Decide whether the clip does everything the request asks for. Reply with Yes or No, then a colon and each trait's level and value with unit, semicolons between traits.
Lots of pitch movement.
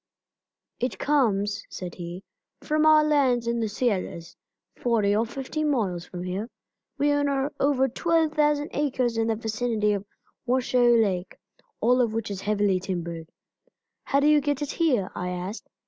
Yes: wide, 5.9 semitones